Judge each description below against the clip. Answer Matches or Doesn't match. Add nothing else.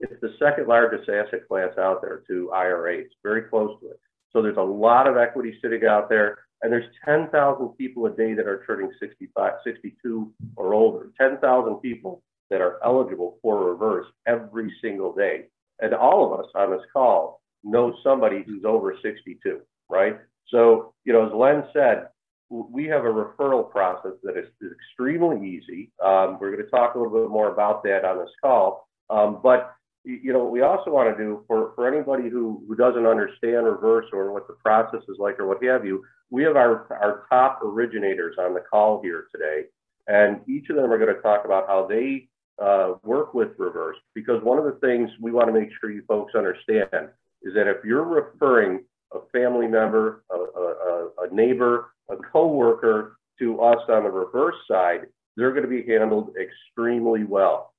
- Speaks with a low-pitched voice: Matches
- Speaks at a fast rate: Doesn't match